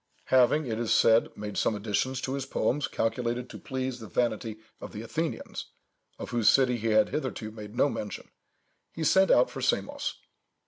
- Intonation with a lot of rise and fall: No, average, 3.3 semitones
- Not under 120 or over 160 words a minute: No, average, 180 wpm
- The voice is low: Yes, low, 120 Hz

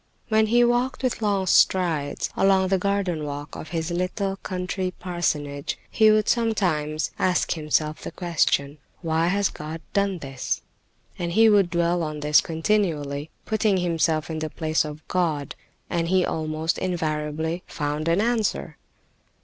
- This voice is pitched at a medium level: Yes, medium, 170 Hz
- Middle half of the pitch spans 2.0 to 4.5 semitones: Yes, average, 3.9 semitones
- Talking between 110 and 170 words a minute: Yes, average, 150 wpm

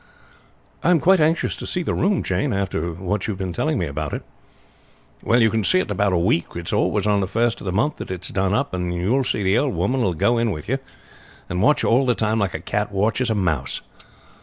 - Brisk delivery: Yes, fast, 265 wpm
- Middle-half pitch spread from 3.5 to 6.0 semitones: Yes, average, 5.2 semitones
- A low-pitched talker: Yes, low, 105 Hz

